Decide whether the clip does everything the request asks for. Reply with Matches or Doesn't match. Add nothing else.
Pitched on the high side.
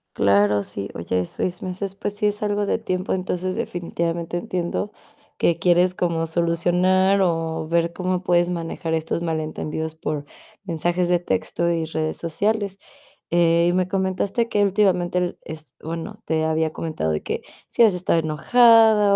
Doesn't match